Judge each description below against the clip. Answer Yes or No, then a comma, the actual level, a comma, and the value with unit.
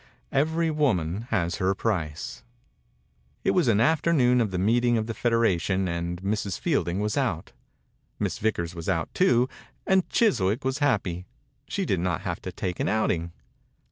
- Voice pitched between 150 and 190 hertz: No, low, 105 Hz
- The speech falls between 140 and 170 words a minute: Yes, average, 165 wpm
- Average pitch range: No, wide, 6.2 semitones